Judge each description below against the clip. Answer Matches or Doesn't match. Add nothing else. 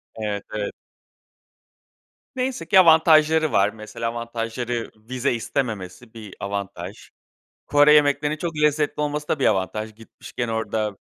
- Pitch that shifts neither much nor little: Doesn't match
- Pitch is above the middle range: Doesn't match